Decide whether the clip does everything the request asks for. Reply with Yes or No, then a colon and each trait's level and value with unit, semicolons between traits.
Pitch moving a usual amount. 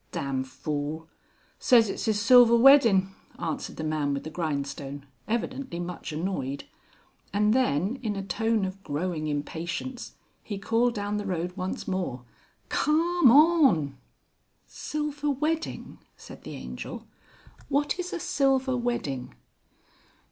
No: wide, 8.8 semitones